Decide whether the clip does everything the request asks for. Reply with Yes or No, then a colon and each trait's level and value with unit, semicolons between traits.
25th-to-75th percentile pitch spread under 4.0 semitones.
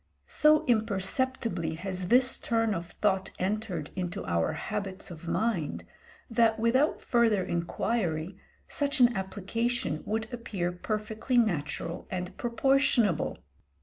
No: average, 4.9 semitones